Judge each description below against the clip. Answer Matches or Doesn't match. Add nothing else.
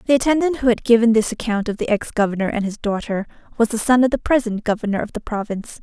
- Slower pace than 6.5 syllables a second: Doesn't match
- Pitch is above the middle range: Matches